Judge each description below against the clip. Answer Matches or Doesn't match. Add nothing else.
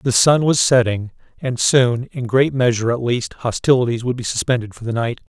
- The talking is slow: Doesn't match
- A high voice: Doesn't match